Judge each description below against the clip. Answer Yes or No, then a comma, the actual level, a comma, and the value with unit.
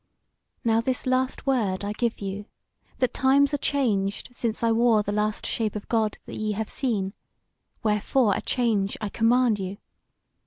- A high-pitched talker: Yes, high, 225 Hz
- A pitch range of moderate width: Yes, average, 3.2 semitones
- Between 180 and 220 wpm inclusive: No, average, 165 wpm